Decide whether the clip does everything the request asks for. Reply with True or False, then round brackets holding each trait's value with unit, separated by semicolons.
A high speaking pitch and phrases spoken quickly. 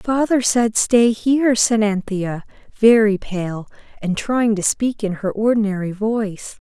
False (215 Hz; 145 wpm)